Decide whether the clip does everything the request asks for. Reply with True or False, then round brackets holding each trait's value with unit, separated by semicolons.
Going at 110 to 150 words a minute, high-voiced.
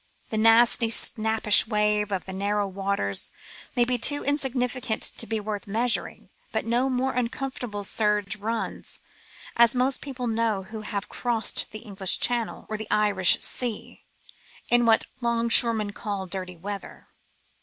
True (145 wpm; 220 Hz)